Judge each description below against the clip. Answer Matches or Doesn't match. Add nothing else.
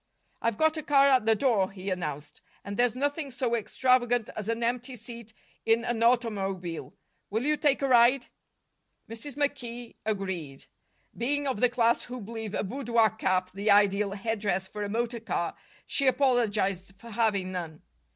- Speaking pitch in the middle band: Doesn't match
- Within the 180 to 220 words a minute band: Doesn't match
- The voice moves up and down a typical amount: Matches